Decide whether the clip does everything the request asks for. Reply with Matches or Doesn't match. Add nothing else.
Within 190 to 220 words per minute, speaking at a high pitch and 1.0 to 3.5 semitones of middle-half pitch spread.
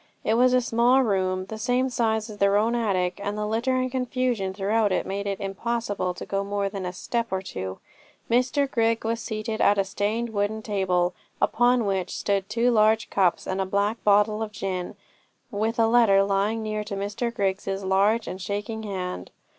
Matches